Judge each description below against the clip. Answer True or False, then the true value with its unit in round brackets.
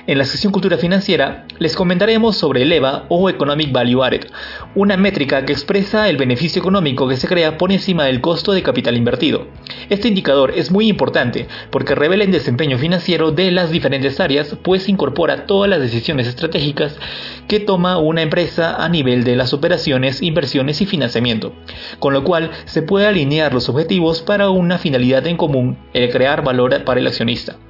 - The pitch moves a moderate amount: False (5.7 semitones)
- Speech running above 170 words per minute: True (180 wpm)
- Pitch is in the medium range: True (165 Hz)